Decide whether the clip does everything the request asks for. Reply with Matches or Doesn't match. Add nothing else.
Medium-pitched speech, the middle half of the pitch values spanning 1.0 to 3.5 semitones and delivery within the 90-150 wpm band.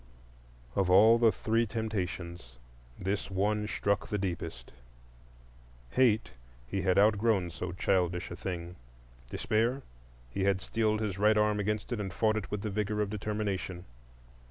Doesn't match